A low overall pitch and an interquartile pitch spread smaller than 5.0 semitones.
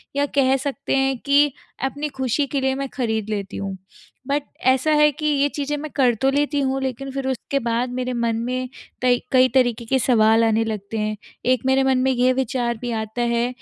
No: very high, 255 Hz; narrow, 2.6 semitones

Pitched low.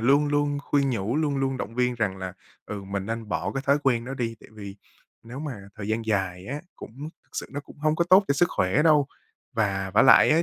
Yes: low, 125 Hz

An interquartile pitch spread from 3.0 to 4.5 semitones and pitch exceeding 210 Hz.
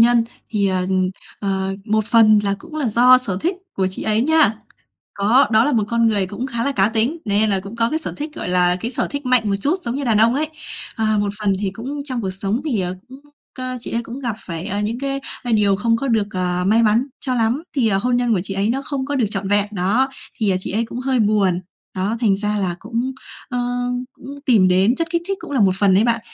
Yes: average, 4.2 semitones; high, 225 Hz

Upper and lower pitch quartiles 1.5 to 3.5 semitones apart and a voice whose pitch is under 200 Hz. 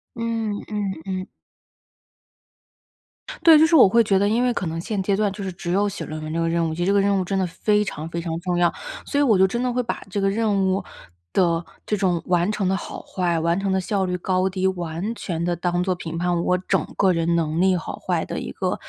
Yes: average, 2.8 semitones; high, 190 Hz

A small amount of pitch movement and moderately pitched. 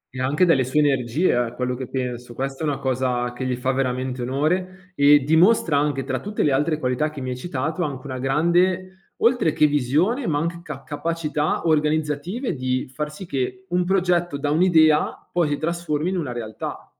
No: average, 4.7 semitones; medium, 150 Hz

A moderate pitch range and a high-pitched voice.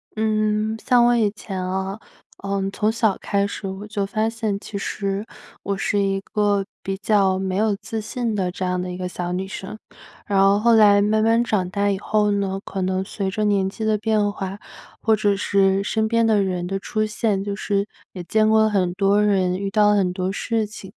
No: narrow, 1.9 semitones; high, 200 Hz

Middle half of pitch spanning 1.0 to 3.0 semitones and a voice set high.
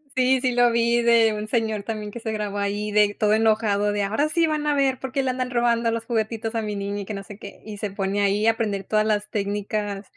Yes: narrow, 2.4 semitones; high, 215 Hz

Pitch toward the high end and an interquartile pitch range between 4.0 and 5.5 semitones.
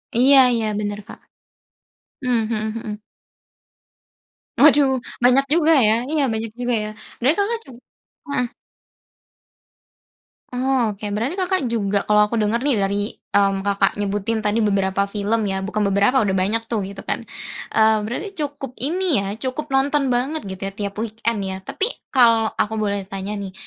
Yes: high, 225 Hz; average, 4.8 semitones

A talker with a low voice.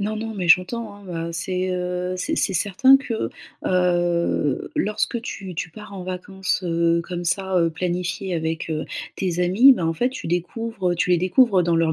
No: medium, 180 Hz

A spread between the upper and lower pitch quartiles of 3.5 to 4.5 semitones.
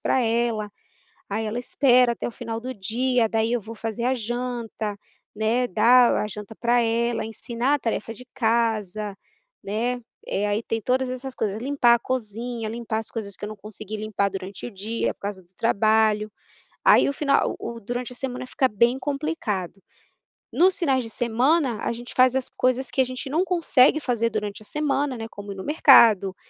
No: average, 2.9 semitones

